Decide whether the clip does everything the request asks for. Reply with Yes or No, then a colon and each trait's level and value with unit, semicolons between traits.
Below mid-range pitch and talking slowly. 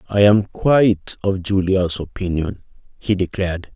Yes: very low, 95 Hz; slow, 130 wpm